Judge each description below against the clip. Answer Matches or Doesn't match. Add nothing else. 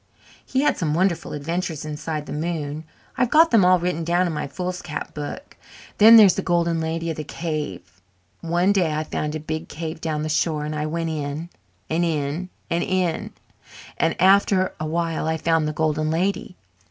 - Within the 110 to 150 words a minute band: Doesn't match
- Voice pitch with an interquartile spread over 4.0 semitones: Doesn't match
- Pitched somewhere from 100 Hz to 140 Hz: Doesn't match